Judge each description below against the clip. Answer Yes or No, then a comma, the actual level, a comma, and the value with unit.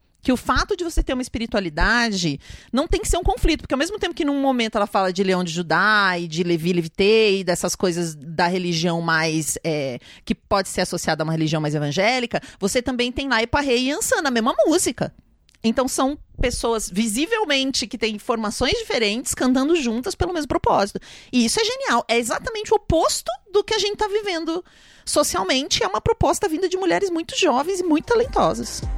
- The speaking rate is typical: No, fast, 195 wpm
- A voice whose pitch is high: Yes, very high, 250 Hz